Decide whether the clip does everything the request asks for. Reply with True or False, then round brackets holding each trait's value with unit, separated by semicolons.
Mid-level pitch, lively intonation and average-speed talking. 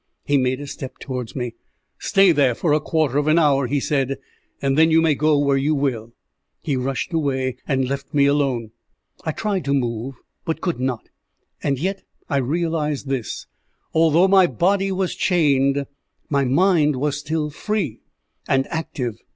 False (145 Hz; 3.3 semitones; 170 wpm)